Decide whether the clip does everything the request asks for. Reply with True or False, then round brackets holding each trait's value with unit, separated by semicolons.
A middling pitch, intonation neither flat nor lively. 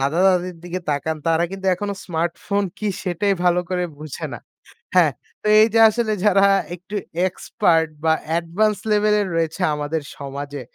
True (180 Hz; 3.9 semitones)